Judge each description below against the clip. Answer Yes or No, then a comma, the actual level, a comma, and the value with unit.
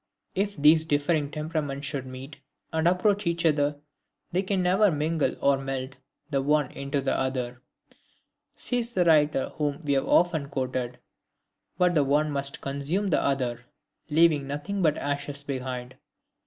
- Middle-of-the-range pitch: Yes, medium, 145 Hz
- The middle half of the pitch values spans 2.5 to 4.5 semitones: Yes, average, 3.3 semitones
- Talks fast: No, average, 155 wpm